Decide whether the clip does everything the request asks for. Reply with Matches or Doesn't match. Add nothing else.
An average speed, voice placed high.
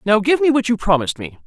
Doesn't match